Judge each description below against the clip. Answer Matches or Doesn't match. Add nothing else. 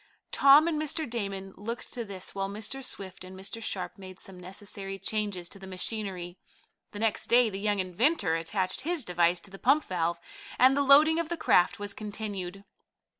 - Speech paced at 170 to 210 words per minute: Matches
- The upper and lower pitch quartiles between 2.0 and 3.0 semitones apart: Doesn't match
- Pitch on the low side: Doesn't match